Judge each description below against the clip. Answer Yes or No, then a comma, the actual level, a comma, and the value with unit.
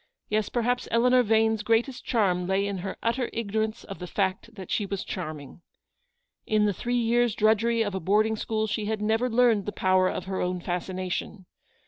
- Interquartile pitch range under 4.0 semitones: Yes, average, 3.2 semitones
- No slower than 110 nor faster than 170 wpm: No, average, 185 wpm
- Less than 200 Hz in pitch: No, high, 215 Hz